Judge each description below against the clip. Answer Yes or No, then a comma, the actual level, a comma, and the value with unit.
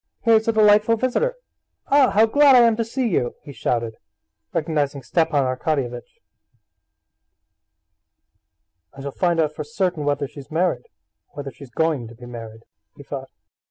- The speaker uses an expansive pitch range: Yes, wide, 8.6 semitones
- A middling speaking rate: Yes, average, 155 wpm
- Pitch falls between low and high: Yes, medium, 155 Hz